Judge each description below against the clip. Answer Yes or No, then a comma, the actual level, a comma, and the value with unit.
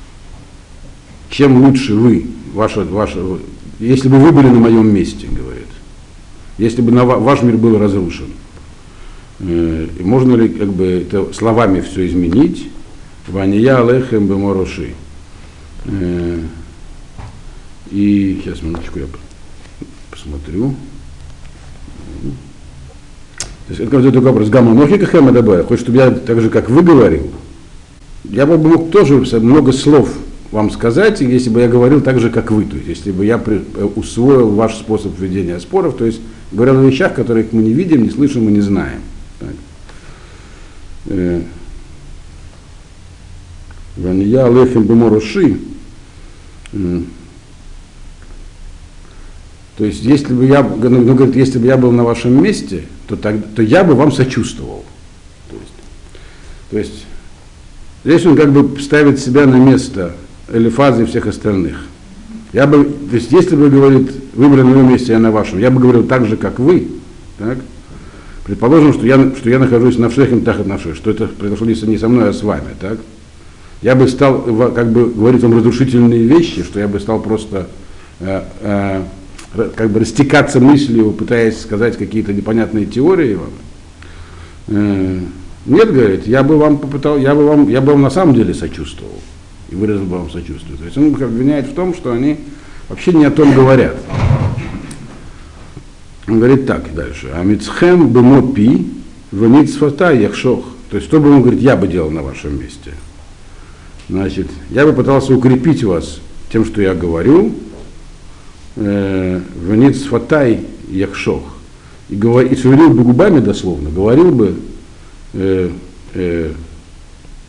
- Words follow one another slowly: No, average, 140 wpm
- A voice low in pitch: Yes, low, 105 Hz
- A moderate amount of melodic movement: No, wide, 6.4 semitones